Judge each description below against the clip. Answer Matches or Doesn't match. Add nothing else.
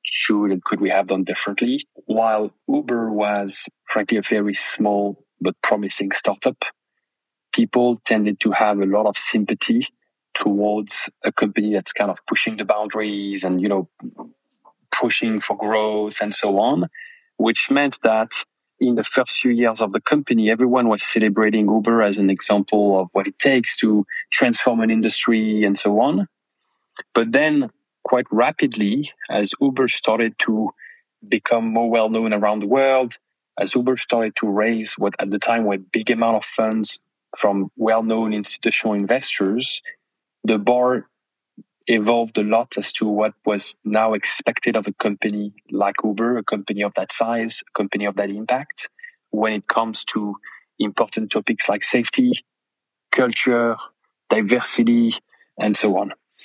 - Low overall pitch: Matches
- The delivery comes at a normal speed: Matches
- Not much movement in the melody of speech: Matches